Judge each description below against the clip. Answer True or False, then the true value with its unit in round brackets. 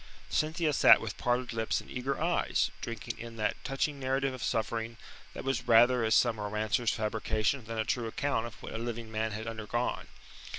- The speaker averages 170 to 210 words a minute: True (185 wpm)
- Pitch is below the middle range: True (115 Hz)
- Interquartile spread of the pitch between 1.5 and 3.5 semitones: True (2.6 semitones)